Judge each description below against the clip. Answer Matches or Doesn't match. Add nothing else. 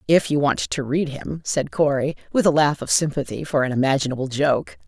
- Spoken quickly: Matches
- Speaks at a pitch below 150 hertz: Matches